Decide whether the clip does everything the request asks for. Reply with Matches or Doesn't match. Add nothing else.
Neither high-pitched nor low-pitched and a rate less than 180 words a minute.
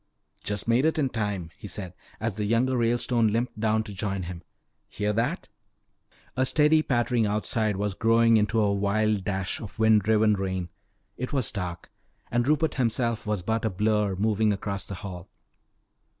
Doesn't match